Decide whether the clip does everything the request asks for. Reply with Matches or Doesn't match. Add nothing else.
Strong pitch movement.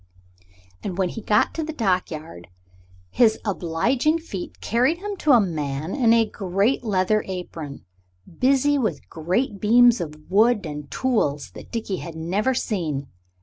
Matches